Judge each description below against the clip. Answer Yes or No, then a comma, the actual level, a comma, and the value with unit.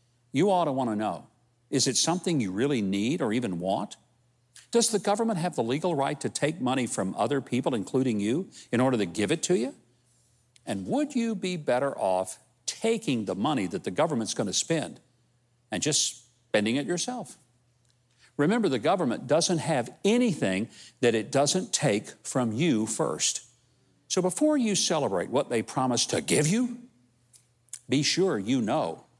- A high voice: No, low, 130 Hz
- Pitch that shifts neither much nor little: No, wide, 6.9 semitones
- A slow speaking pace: No, average, 175 wpm